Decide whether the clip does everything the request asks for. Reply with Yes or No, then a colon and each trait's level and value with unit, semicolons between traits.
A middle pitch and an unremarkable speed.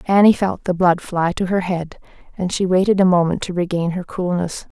No: medium, 180 Hz; fast, 215 wpm